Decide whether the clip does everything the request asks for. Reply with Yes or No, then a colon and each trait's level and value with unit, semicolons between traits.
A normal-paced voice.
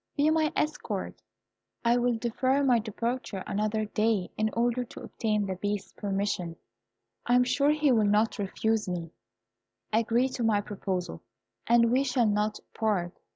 Yes: average, 155 wpm